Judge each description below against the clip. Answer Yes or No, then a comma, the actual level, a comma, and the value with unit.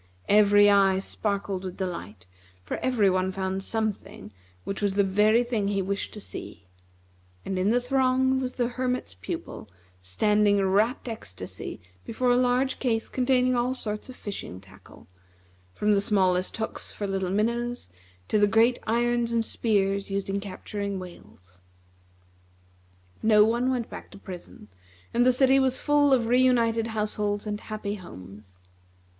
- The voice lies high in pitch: Yes, high, 210 Hz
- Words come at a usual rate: Yes, average, 155 wpm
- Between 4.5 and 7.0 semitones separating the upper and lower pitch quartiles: No, average, 3.9 semitones